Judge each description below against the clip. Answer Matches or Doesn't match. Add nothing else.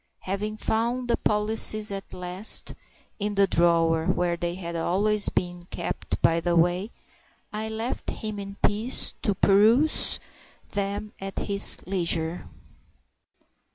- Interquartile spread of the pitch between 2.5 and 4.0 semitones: Matches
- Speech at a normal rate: Doesn't match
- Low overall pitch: Doesn't match